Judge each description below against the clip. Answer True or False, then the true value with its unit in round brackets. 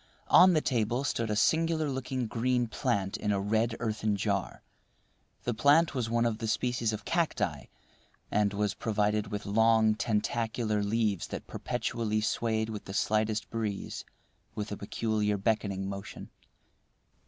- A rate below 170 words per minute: True (145 wpm)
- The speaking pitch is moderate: False (110 Hz)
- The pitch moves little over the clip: True (2.2 semitones)